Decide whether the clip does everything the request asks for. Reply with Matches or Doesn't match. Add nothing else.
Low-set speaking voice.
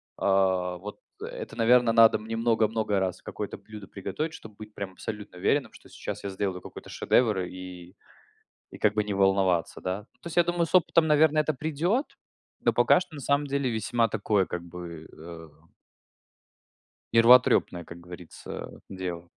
Matches